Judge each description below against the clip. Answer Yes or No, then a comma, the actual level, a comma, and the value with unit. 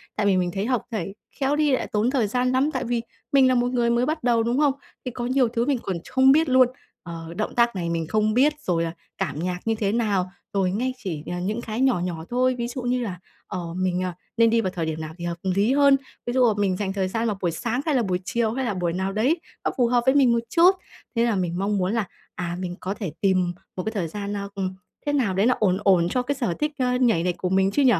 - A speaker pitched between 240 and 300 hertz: No, high, 215 Hz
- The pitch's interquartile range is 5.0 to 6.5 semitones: Yes, average, 5.3 semitones